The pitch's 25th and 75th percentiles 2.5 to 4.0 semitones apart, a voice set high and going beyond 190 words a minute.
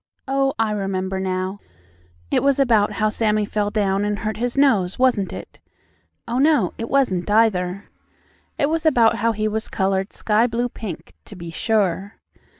No: average, 3.6 semitones; high, 215 Hz; average, 165 wpm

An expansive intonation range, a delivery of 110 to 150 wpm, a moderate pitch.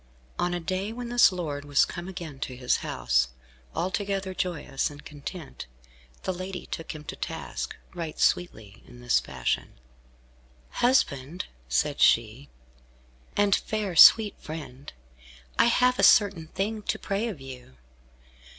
Yes: wide, 6.2 semitones; average, 140 wpm; medium, 170 Hz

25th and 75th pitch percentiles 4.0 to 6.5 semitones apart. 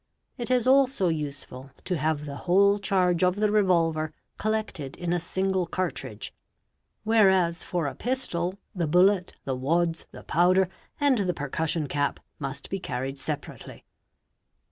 Yes: average, 4.3 semitones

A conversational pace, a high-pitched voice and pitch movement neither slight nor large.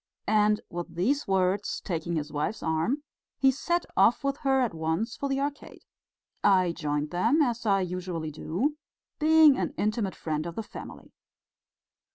No: average, 160 wpm; high, 200 Hz; wide, 8.0 semitones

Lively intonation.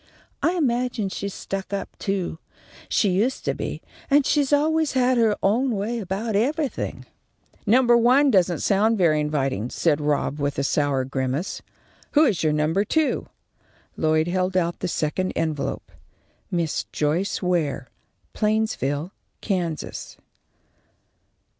Yes: wide, 7.3 semitones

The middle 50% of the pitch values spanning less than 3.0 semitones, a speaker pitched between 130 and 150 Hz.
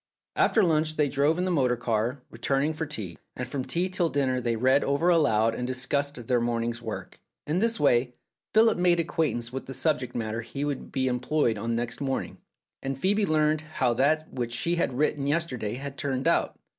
No: average, 4.3 semitones; low, 135 Hz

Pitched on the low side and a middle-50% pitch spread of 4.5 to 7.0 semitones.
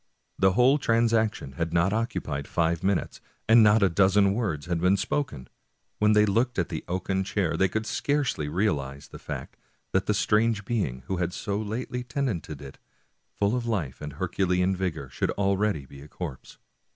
Yes: very low, 95 Hz; average, 4.8 semitones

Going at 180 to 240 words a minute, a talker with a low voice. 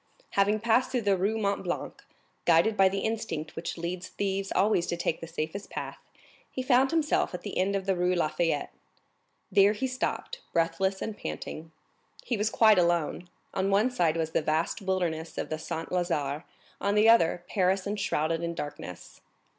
No: average, 185 wpm; medium, 185 Hz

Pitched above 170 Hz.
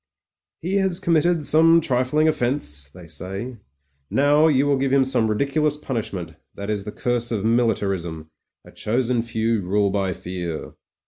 No: low, 120 Hz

